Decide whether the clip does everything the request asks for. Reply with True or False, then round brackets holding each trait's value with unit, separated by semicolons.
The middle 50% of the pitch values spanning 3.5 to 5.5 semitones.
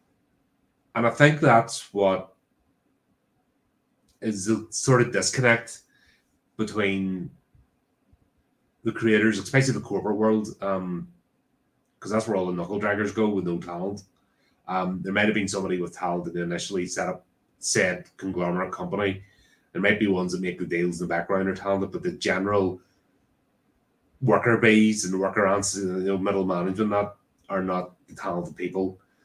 False (2.8 semitones)